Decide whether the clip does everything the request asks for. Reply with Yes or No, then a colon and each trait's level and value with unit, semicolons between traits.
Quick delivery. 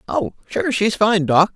No: average, 195 wpm